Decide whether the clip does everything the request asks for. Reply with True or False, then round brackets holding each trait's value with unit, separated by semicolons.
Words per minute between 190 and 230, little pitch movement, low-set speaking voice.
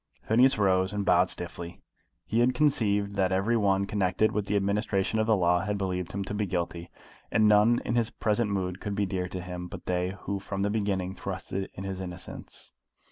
True (205 wpm; 2.3 semitones; 100 Hz)